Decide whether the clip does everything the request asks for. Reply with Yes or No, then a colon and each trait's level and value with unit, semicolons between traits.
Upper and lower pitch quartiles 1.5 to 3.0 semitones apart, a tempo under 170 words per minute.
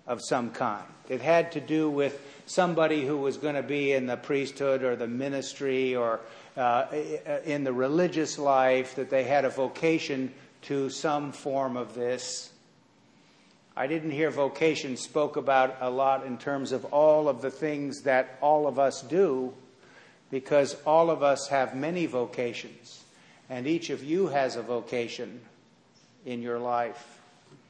Yes: narrow, 2.6 semitones; average, 160 wpm